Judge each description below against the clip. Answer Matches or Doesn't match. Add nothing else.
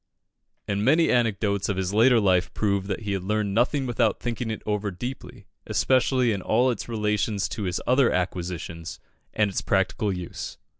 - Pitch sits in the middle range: Doesn't match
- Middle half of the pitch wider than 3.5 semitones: Matches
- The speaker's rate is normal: Matches